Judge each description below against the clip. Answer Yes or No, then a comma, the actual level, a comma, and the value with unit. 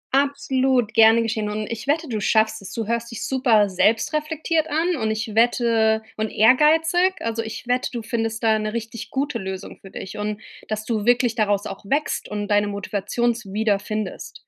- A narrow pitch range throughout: No, average, 3.0 semitones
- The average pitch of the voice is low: No, high, 225 Hz